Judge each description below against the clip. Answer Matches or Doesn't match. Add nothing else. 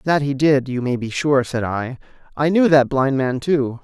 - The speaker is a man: Matches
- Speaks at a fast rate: Matches